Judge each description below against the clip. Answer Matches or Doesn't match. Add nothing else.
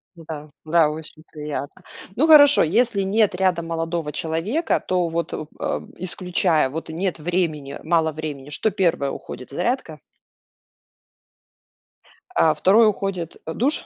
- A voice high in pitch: Doesn't match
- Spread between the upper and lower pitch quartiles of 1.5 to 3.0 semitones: Doesn't match